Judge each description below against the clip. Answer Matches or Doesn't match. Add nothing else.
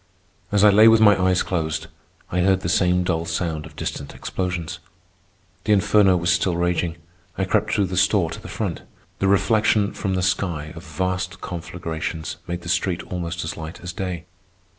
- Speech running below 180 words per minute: Doesn't match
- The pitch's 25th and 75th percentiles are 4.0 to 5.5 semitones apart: Doesn't match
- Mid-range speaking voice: Doesn't match